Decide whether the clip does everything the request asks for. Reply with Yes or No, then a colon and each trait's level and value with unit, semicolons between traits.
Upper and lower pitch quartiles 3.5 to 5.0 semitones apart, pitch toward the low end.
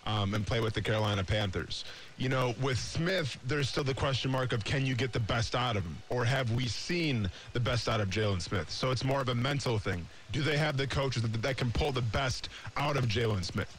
Yes: average, 3.9 semitones; low, 120 Hz